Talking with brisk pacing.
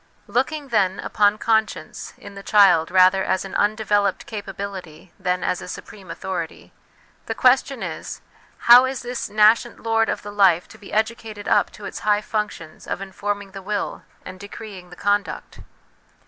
No: average, 165 wpm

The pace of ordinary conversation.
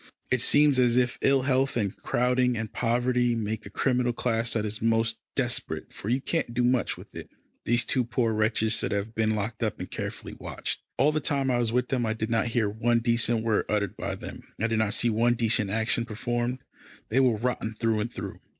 No: fast, 225 wpm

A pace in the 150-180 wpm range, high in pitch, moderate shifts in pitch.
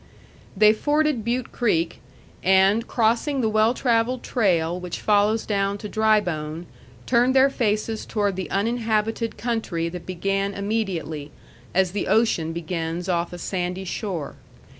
No: slow, 135 wpm; high, 205 Hz; average, 4.2 semitones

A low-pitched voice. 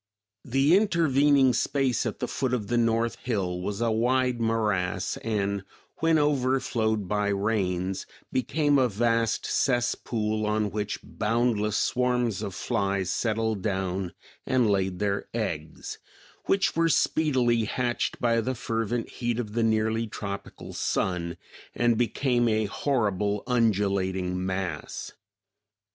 Yes: low, 110 Hz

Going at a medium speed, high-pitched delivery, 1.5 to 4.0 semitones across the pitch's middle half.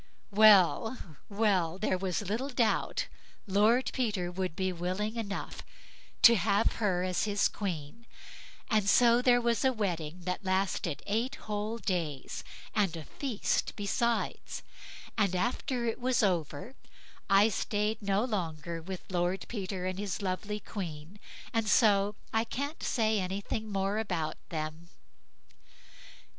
No: slow, 130 wpm; high, 200 Hz; average, 3.5 semitones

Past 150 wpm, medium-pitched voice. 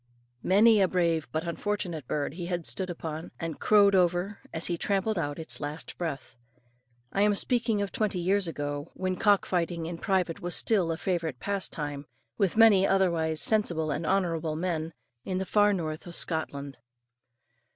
Yes: average, 170 wpm; medium, 175 Hz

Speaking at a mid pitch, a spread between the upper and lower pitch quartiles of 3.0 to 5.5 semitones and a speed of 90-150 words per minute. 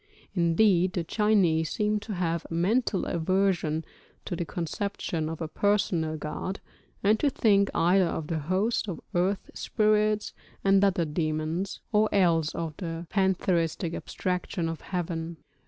Yes: medium, 180 Hz; average, 3.5 semitones; average, 140 wpm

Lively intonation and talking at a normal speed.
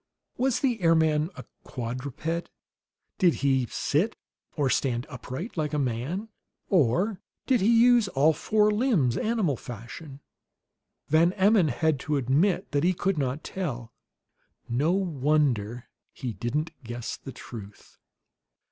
No: wide, 6.6 semitones; slow, 130 wpm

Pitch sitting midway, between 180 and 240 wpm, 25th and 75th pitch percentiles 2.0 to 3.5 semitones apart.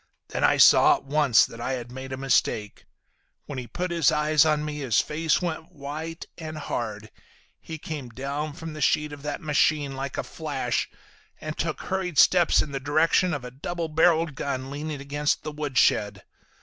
Yes: medium, 150 Hz; average, 185 wpm; average, 2.8 semitones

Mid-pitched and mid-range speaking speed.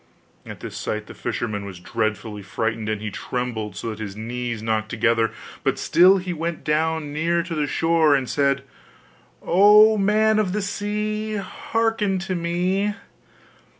Yes: medium, 155 Hz; average, 155 wpm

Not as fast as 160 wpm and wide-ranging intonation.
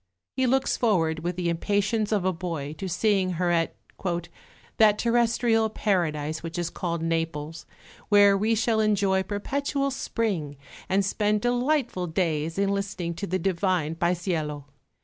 No: average, 145 wpm; average, 4.5 semitones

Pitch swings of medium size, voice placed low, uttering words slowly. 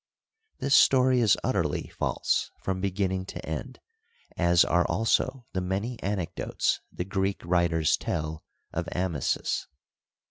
Yes: average, 3.0 semitones; very low, 95 Hz; slow, 120 wpm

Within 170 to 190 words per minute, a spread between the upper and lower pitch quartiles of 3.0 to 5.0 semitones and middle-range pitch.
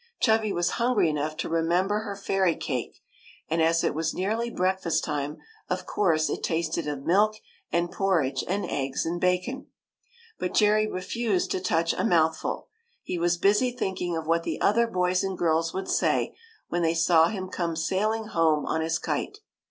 Yes: average, 175 wpm; average, 3.5 semitones; medium, 175 Hz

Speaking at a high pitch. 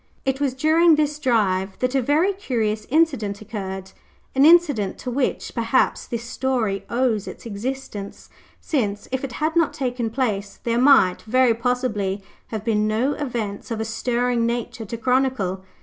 Yes: high, 240 Hz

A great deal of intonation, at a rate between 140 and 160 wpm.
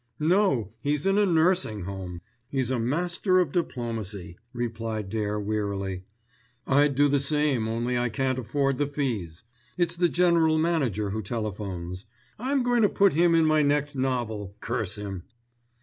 Yes: wide, 7.0 semitones; average, 155 wpm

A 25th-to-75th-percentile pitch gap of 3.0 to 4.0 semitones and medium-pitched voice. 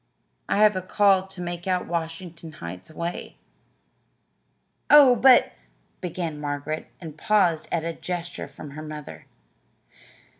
Yes: average, 3.3 semitones; medium, 170 Hz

